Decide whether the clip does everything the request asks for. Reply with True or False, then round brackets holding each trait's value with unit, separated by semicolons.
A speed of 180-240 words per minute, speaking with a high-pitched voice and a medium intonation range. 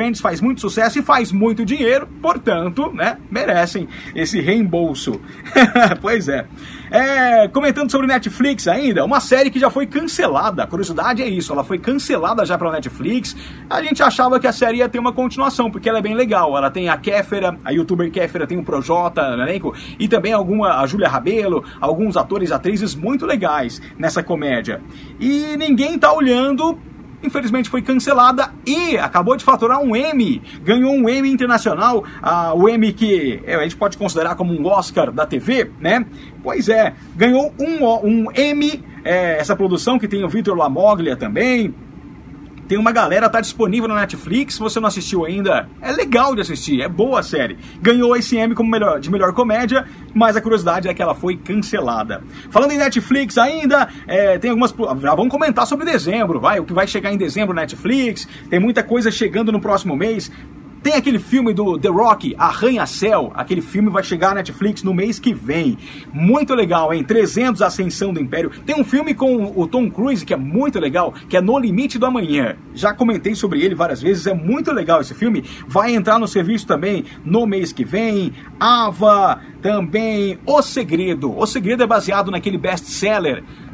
True (185 wpm; 220 Hz; 5.0 semitones)